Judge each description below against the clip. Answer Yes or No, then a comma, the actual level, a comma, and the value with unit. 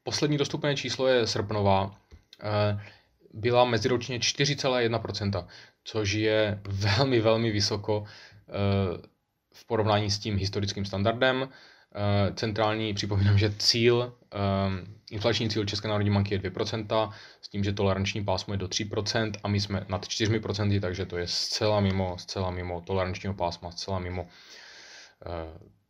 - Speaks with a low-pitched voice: Yes, low, 105 Hz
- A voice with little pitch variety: Yes, narrow, 2.3 semitones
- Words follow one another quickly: No, average, 125 wpm